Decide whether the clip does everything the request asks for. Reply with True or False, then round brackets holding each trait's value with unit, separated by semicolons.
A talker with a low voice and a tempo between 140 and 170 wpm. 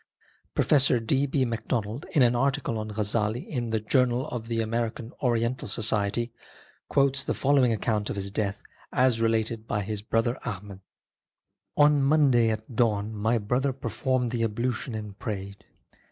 True (115 Hz; 160 wpm)